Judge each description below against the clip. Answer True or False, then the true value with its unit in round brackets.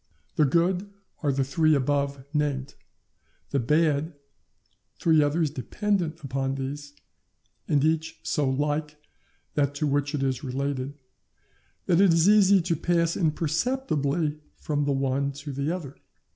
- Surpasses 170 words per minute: False (135 wpm)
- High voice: False (145 Hz)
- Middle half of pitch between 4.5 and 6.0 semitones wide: False (2.8 semitones)